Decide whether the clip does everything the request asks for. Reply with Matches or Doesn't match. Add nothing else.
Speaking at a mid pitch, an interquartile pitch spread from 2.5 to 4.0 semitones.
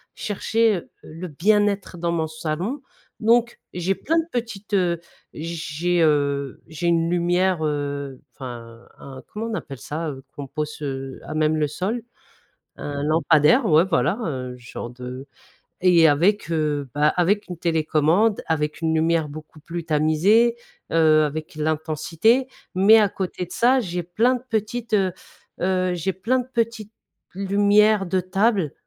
Doesn't match